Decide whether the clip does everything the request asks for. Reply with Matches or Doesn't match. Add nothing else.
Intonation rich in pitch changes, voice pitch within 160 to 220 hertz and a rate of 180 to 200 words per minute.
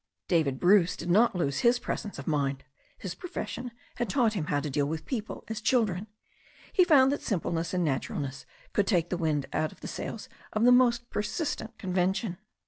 Matches